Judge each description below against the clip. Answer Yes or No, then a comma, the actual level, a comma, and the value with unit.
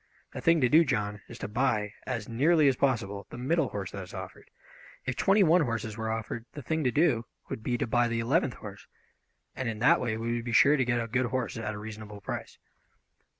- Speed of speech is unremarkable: No, fast, 235 wpm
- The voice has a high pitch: No, low, 120 Hz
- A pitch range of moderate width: Yes, average, 3.4 semitones